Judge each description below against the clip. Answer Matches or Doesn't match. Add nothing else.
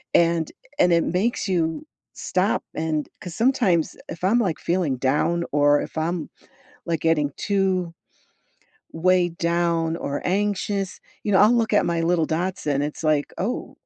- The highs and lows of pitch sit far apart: Doesn't match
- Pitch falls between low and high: Matches